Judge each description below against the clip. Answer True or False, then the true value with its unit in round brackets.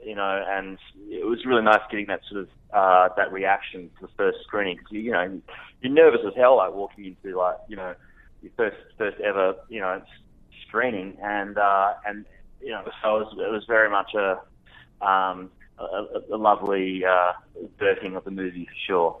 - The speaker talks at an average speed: True (195 wpm)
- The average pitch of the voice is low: True (100 Hz)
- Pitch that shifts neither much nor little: False (2.3 semitones)